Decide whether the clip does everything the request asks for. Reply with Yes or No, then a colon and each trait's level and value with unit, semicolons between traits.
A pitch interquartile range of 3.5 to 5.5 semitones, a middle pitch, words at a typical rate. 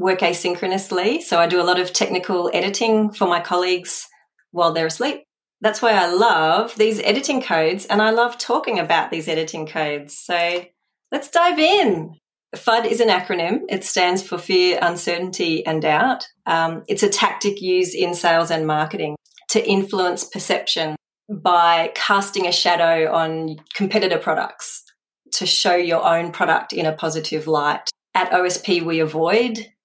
Yes: average, 3.8 semitones; medium, 180 Hz; average, 155 wpm